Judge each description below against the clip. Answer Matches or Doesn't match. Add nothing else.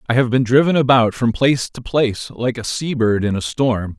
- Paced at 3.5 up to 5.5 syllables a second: Matches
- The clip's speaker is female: Doesn't match